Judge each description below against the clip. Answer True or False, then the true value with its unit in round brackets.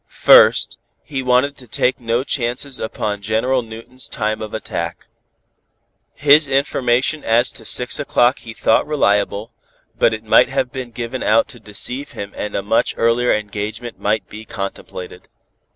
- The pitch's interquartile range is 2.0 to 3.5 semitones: True (3.1 semitones)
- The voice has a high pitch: False (120 Hz)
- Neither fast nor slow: True (150 wpm)